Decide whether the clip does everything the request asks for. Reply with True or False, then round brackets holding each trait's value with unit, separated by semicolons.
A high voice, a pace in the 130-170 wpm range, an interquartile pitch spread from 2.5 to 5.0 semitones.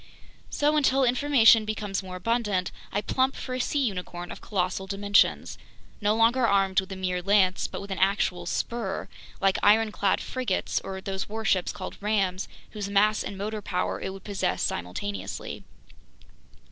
True (200 Hz; 160 wpm; 2.8 semitones)